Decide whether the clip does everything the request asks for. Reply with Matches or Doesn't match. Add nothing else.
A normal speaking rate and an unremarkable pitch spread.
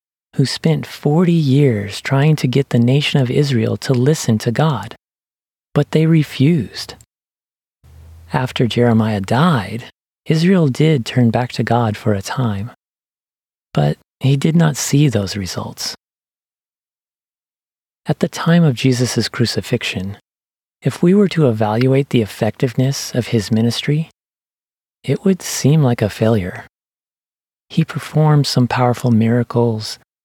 Doesn't match